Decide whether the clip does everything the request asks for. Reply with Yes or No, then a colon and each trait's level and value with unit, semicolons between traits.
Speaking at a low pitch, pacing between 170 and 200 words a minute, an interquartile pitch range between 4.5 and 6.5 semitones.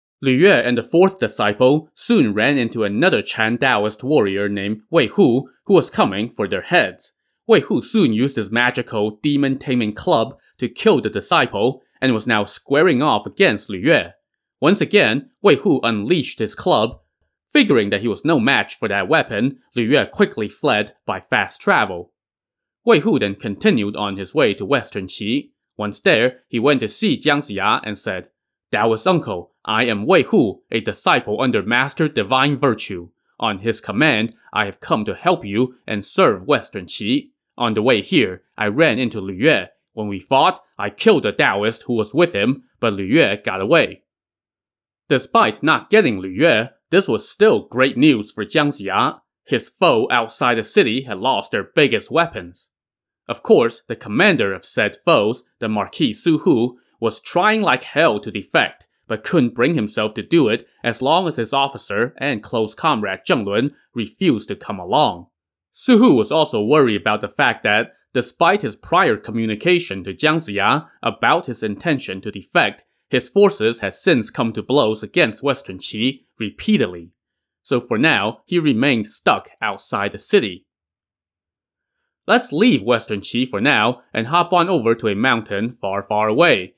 Yes: low, 115 Hz; average, 175 wpm; wide, 5.6 semitones